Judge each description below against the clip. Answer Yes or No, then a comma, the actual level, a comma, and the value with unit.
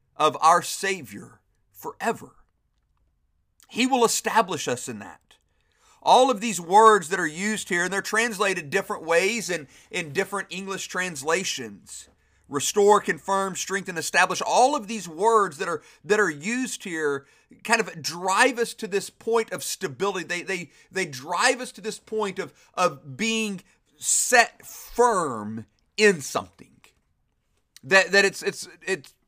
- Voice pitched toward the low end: No, high, 195 Hz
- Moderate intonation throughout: Yes, average, 4.2 semitones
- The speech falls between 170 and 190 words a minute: No, average, 150 wpm